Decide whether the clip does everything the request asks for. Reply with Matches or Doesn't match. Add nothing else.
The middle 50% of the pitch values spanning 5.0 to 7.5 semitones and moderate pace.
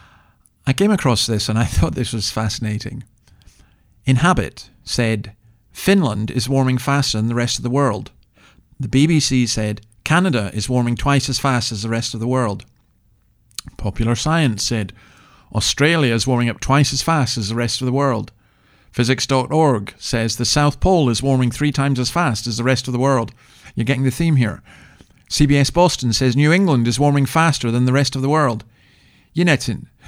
Doesn't match